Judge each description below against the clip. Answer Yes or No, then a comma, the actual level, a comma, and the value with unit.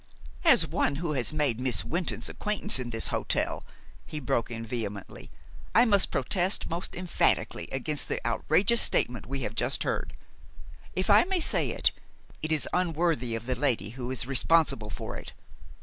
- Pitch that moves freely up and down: Yes, wide, 6.5 semitones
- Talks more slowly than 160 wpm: No, average, 165 wpm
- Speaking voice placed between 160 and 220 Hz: No, medium, 140 Hz